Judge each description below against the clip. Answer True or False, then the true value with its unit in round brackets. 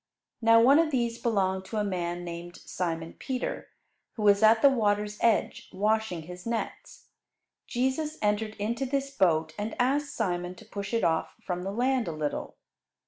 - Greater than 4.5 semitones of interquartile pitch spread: True (5.0 semitones)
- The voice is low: False (210 Hz)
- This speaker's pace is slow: False (170 wpm)